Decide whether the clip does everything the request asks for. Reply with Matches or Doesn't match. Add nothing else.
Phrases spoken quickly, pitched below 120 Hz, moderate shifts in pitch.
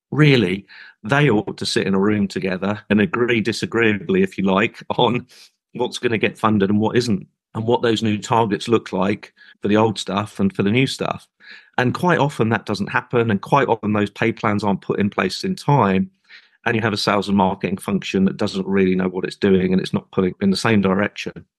Matches